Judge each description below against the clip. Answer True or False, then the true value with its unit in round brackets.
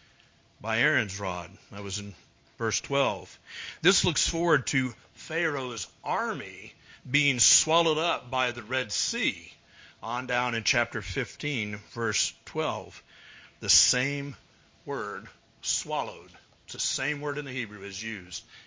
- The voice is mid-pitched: False (125 Hz)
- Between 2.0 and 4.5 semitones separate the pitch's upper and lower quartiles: False (5.1 semitones)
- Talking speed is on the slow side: True (130 wpm)